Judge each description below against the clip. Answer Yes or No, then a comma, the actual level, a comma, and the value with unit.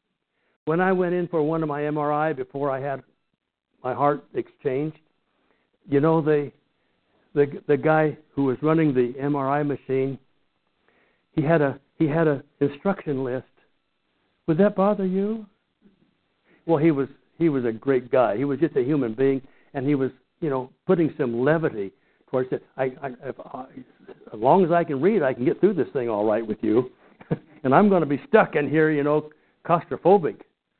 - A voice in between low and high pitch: Yes, medium, 145 Hz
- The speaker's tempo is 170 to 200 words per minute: Yes, average, 185 wpm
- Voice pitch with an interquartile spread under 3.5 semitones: Yes, average, 3.1 semitones